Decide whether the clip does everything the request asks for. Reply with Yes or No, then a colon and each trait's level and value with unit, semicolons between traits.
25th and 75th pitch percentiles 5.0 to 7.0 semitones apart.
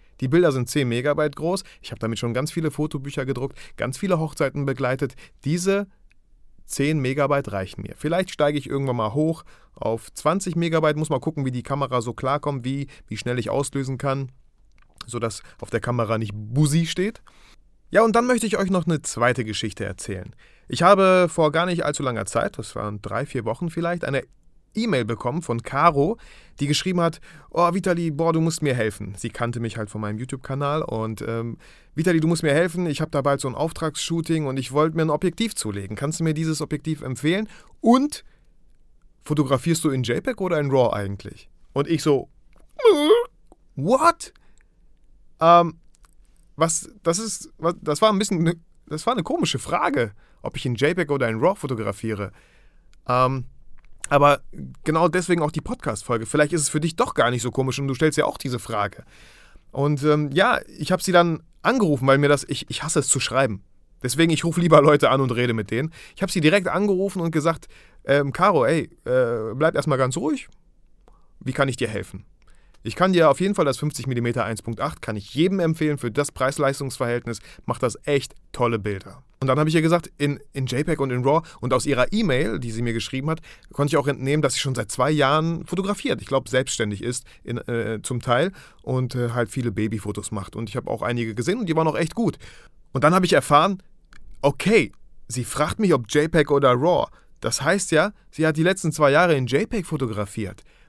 Yes: wide, 5.4 semitones